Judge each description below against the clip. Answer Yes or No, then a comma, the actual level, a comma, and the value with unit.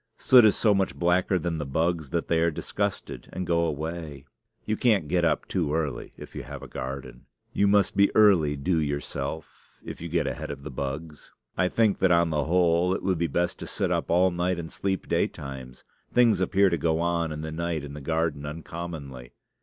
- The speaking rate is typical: No, fast, 210 wpm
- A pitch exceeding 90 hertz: No, very low, 85 Hz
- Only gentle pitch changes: No, average, 3.4 semitones